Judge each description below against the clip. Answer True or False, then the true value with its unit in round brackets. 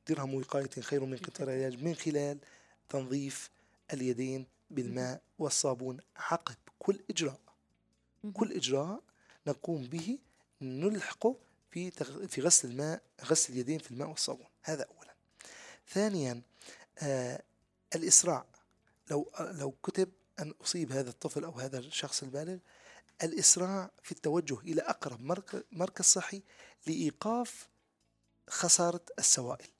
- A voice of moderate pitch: True (150 Hz)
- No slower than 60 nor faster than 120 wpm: True (110 wpm)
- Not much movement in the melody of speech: False (5.5 semitones)